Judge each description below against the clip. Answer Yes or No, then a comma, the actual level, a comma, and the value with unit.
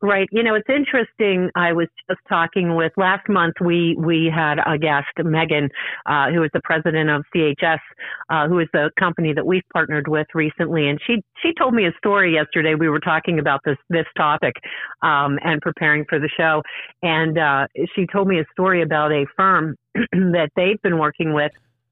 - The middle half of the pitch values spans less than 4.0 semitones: Yes, average, 3.2 semitones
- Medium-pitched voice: Yes, medium, 165 Hz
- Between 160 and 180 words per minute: No, average, 195 wpm